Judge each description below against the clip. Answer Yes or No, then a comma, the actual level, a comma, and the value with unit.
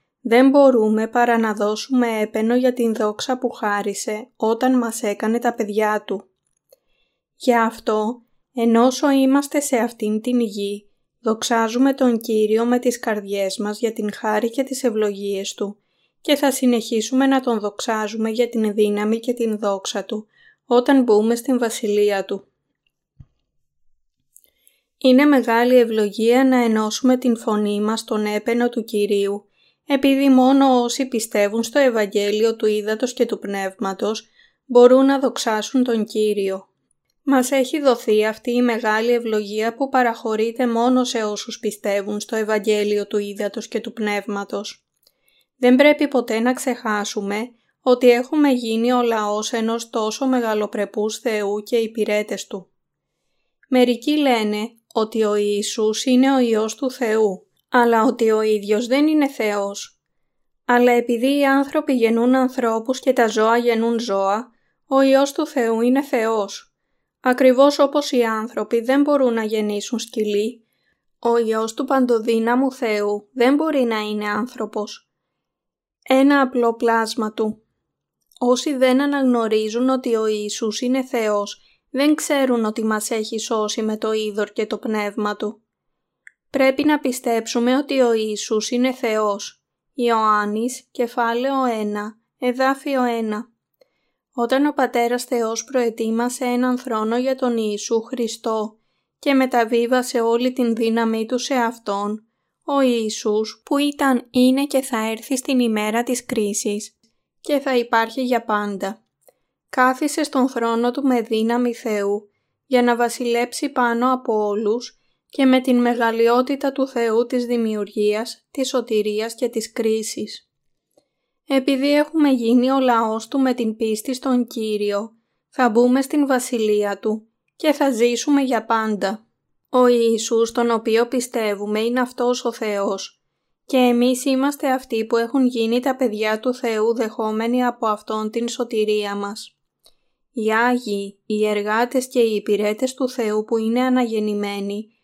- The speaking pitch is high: Yes, high, 230 Hz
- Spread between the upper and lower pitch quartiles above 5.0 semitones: No, average, 2.9 semitones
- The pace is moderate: Yes, average, 140 wpm